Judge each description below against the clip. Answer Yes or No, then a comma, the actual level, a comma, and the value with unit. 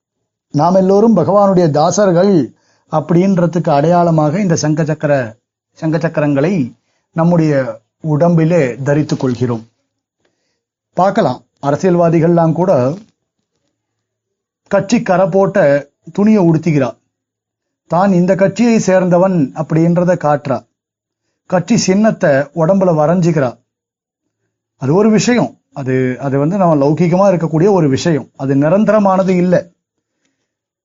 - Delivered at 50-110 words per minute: Yes, average, 90 wpm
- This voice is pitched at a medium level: Yes, medium, 165 Hz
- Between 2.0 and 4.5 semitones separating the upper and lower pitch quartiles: No, average, 5.1 semitones